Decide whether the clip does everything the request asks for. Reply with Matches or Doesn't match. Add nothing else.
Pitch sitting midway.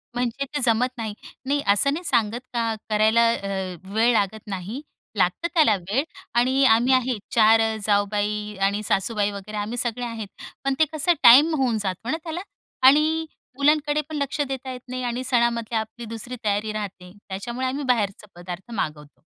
Doesn't match